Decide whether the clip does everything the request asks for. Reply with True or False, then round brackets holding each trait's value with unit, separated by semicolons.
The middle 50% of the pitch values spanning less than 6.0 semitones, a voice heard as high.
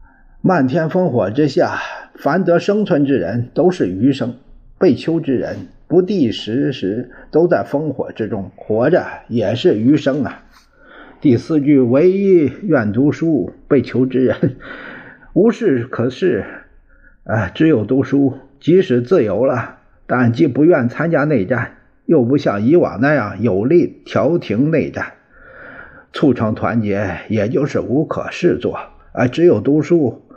False (5.3 semitones; 140 Hz)